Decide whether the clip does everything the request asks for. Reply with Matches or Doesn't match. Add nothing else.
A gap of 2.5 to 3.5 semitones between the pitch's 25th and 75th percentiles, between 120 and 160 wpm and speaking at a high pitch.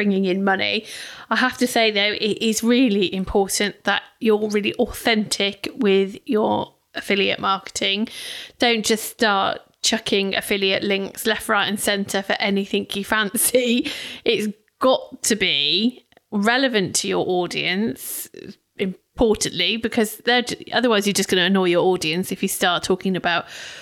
Matches